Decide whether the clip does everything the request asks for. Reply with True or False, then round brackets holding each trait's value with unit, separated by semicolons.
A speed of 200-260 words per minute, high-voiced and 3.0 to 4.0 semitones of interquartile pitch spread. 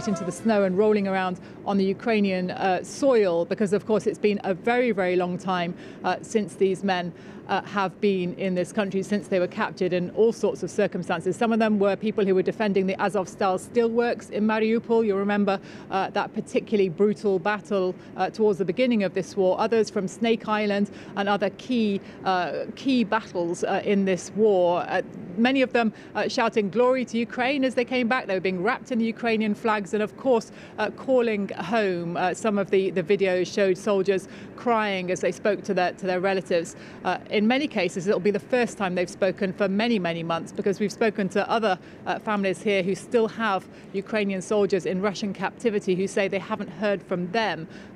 False (205 wpm; 200 Hz; 2.4 semitones)